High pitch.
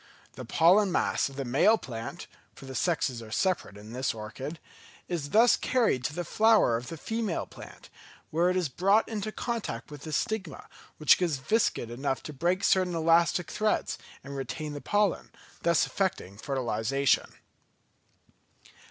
No: medium, 160 Hz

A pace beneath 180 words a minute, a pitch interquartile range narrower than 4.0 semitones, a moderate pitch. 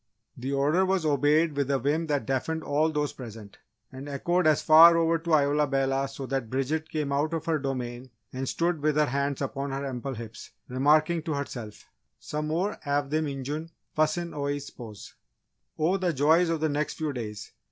No: average, 185 wpm; average, 2.8 semitones; medium, 145 Hz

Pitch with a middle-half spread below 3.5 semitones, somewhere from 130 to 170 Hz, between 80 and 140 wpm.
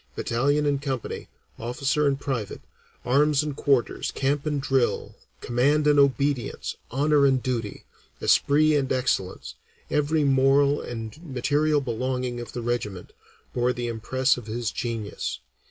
Yes: average, 3.0 semitones; low, 135 Hz; slow, 135 wpm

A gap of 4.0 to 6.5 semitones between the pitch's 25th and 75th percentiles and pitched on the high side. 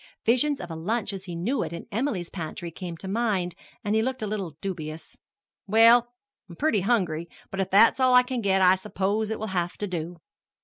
Yes: average, 4.6 semitones; high, 195 Hz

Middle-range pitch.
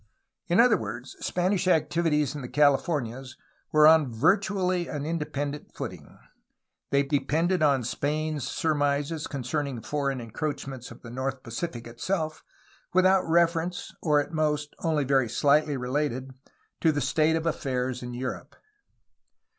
Yes: medium, 145 Hz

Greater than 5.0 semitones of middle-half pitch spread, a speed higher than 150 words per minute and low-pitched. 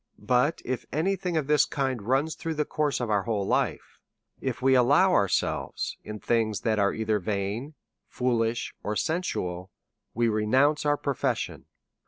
Yes: wide, 5.4 semitones; average, 165 wpm; low, 125 Hz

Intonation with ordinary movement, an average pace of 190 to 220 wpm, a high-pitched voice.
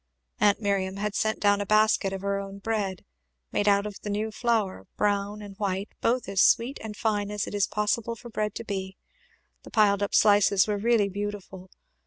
No: narrow, 1.3 semitones; average, 200 wpm; high, 205 Hz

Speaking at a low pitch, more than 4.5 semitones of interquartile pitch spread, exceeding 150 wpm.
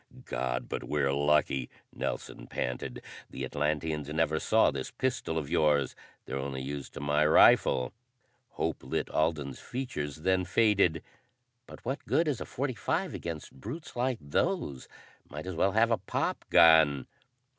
No: very low, 75 Hz; average, 4.9 semitones; average, 145 wpm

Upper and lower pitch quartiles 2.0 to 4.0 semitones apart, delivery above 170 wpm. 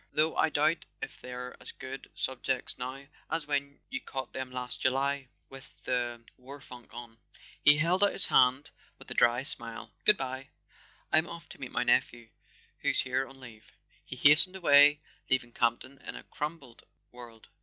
Yes: average, 2.9 semitones; average, 180 wpm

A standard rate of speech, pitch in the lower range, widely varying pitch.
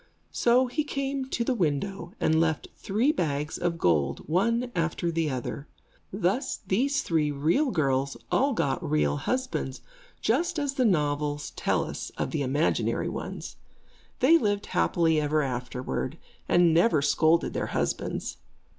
No: average, 145 wpm; medium, 170 Hz; wide, 8.6 semitones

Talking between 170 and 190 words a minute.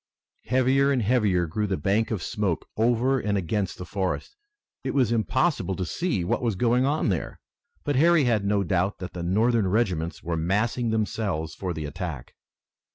Yes: average, 175 wpm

